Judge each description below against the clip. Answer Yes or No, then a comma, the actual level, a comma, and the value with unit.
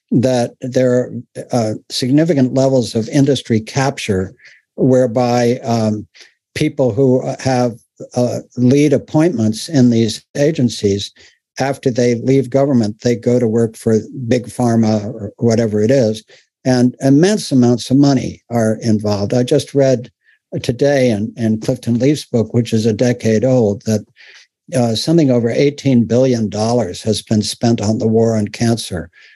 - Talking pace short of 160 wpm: Yes, average, 145 wpm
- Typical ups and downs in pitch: Yes, average, 3.1 semitones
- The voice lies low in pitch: Yes, low, 120 Hz